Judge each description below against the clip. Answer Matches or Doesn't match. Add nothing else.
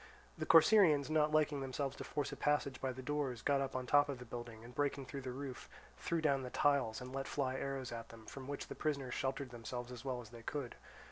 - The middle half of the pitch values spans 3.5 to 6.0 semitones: Doesn't match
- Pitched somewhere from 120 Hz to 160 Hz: Matches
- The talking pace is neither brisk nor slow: Doesn't match